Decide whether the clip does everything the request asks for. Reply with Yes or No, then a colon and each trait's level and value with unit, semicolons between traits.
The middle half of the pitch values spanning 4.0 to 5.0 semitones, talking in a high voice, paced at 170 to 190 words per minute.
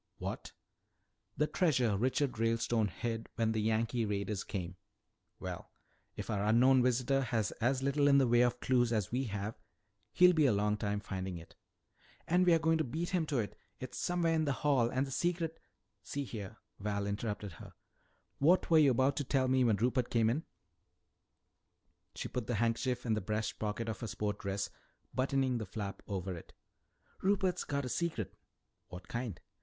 No: average, 4.6 semitones; low, 120 Hz; average, 180 wpm